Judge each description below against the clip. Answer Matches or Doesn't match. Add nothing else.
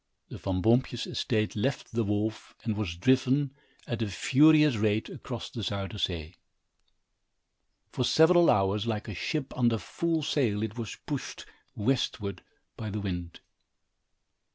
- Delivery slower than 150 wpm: Matches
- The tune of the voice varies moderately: Matches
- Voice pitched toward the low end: Matches